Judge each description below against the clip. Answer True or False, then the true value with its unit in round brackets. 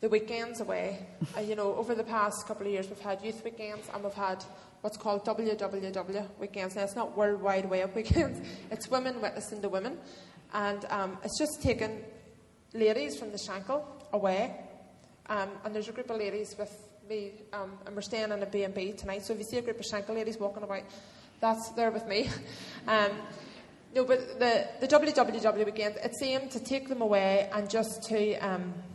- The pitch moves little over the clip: True (1.8 semitones)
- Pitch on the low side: False (210 Hz)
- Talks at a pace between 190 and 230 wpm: True (195 wpm)